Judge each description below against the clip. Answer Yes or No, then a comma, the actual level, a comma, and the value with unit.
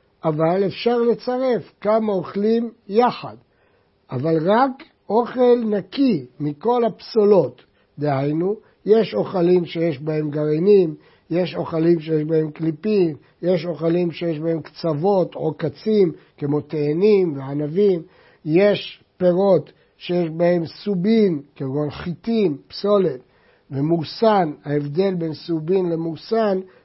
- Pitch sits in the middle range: Yes, medium, 175 Hz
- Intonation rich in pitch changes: No, average, 4.6 semitones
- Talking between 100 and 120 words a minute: Yes, average, 105 wpm